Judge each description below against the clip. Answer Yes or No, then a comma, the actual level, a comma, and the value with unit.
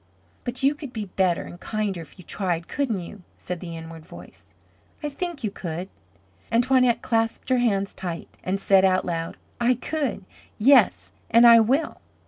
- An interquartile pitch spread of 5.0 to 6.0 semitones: Yes, wide, 5.5 semitones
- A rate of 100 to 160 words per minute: No, average, 175 wpm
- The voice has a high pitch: Yes, high, 210 Hz